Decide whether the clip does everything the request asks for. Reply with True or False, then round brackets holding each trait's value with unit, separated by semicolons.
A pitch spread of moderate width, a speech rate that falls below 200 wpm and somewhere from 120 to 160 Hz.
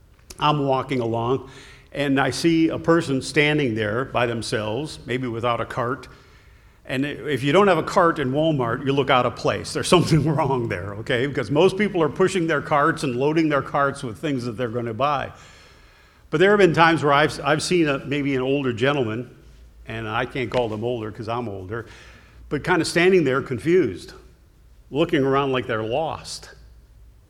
True (4.1 semitones; 190 wpm; 135 Hz)